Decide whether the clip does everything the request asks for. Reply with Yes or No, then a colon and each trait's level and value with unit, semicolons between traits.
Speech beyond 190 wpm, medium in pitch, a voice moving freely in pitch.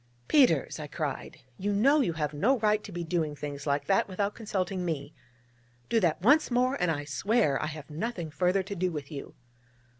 Yes: average, 200 wpm; medium, 180 Hz; wide, 5.8 semitones